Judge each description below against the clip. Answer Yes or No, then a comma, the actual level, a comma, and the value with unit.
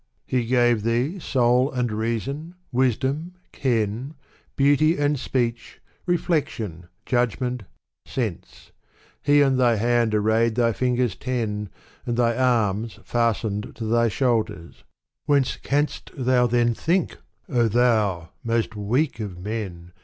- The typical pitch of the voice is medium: No, low, 120 Hz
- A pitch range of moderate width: Yes, average, 3.0 semitones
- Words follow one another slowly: Yes, slow, 125 wpm